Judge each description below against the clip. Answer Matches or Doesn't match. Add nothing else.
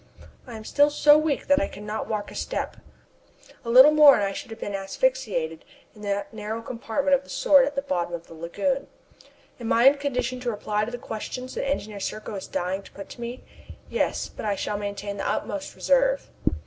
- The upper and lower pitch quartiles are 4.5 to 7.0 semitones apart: Matches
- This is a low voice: Doesn't match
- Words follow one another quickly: Matches